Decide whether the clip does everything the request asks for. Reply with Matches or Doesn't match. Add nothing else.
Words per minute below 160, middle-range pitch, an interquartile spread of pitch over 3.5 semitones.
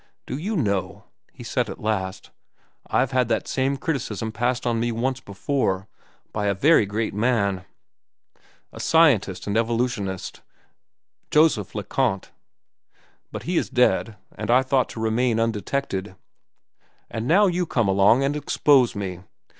Doesn't match